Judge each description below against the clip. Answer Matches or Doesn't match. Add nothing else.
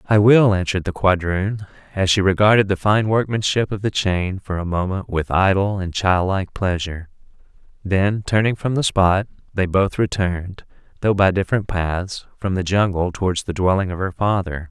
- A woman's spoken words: Doesn't match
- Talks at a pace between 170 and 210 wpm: Matches